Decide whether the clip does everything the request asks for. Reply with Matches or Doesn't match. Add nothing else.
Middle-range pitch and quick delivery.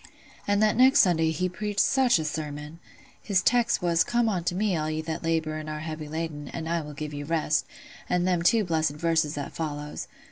Matches